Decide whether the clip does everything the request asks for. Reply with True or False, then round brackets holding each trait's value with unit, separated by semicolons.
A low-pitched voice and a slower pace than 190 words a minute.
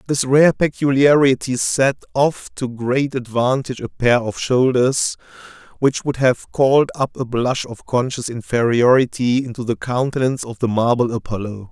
True (125 Hz; 150 wpm)